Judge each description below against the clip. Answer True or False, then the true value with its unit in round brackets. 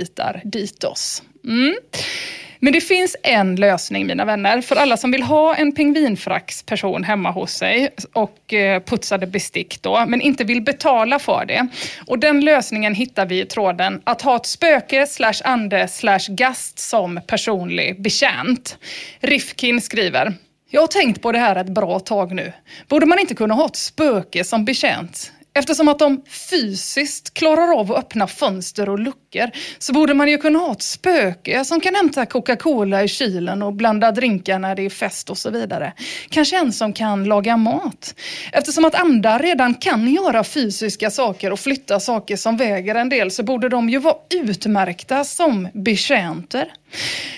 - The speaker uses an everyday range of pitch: False (6.1 semitones)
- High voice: True (240 Hz)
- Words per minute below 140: False (165 wpm)